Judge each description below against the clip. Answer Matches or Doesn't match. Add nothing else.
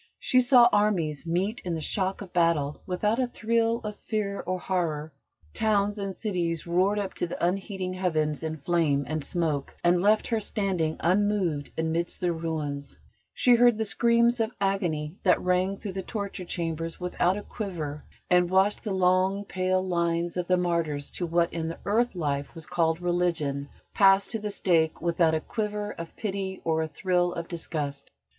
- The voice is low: Doesn't match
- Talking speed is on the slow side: Doesn't match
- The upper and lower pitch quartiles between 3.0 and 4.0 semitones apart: Matches